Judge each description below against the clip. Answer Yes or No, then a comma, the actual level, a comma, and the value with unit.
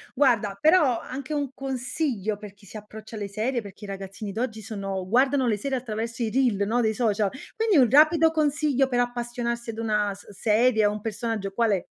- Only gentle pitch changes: No, average, 3.9 semitones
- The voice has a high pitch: Yes, high, 230 Hz